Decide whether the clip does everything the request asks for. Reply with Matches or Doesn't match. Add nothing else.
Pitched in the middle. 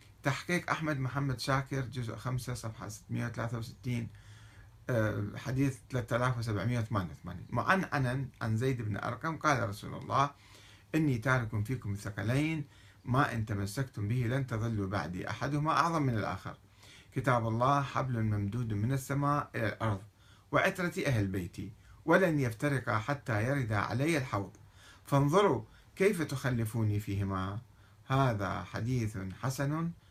Doesn't match